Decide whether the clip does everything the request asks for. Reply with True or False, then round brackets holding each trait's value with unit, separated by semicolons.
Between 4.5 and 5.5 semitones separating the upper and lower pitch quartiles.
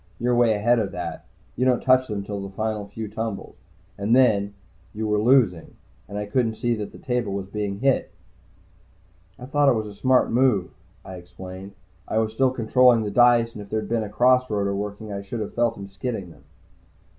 False (3.3 semitones)